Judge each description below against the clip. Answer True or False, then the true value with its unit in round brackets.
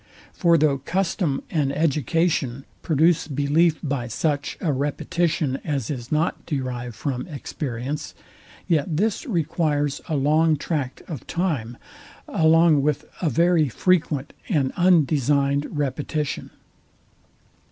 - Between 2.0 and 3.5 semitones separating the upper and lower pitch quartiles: True (3.1 semitones)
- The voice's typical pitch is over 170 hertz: False (150 Hz)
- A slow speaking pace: True (110 wpm)